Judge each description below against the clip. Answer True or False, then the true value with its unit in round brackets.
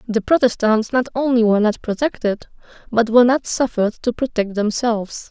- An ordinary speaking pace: True (160 wpm)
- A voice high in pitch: True (230 Hz)